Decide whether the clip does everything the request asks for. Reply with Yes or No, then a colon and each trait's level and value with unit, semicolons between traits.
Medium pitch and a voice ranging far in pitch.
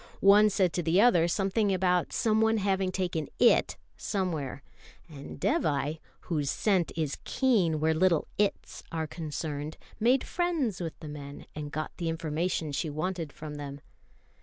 No: medium, 170 Hz; average, 4.4 semitones